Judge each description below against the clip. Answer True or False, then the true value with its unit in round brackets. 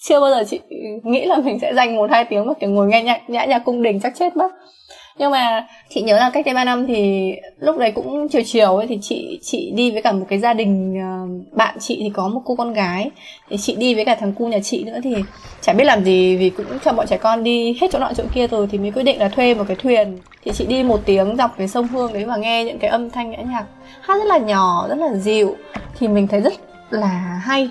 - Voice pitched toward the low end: False (230 Hz)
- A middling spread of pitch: True (3.8 semitones)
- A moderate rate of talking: False (275 wpm)